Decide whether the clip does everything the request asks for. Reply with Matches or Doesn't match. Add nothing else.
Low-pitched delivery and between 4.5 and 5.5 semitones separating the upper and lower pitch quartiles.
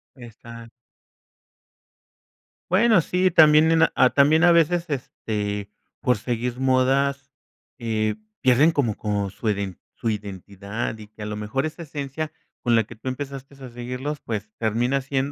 Matches